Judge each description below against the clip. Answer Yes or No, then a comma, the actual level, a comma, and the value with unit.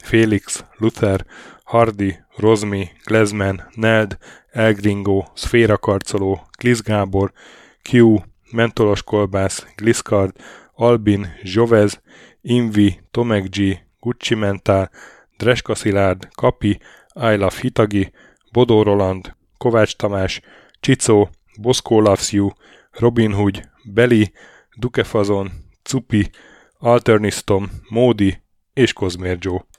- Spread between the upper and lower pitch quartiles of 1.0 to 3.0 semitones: Yes, average, 2.7 semitones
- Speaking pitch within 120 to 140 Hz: No, low, 105 Hz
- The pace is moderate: No, slow, 85 wpm